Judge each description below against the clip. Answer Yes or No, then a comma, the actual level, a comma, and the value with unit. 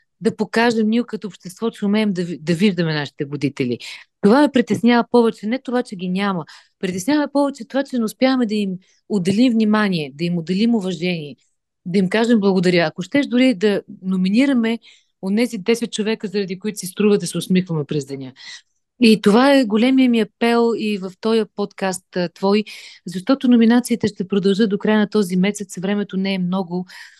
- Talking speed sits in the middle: No, fast, 180 wpm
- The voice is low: No, high, 210 Hz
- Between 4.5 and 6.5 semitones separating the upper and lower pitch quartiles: No, average, 3.8 semitones